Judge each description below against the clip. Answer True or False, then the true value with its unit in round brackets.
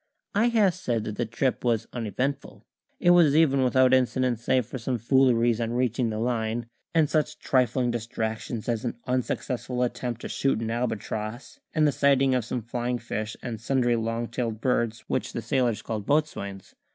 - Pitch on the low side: True (120 Hz)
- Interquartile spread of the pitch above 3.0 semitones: False (2.4 semitones)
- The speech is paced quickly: False (175 wpm)